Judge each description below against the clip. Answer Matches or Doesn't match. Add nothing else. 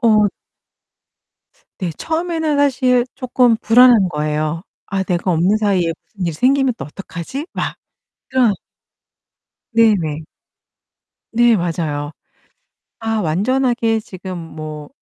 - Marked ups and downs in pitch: Matches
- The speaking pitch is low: Doesn't match